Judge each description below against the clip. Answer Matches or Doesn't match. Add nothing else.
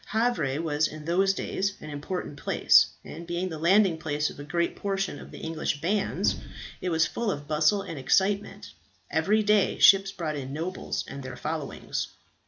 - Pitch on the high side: Doesn't match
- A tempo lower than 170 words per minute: Doesn't match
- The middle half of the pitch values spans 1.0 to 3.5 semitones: Doesn't match